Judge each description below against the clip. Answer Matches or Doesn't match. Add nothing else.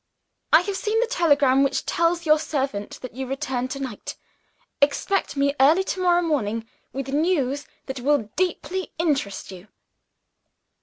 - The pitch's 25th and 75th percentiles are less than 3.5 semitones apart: Doesn't match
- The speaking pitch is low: Doesn't match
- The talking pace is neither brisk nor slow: Matches